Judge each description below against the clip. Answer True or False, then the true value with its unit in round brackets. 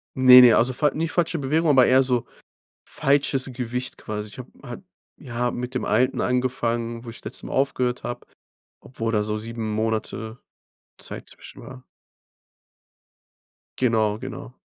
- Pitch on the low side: True (125 Hz)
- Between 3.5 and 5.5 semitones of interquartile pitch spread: False (2.4 semitones)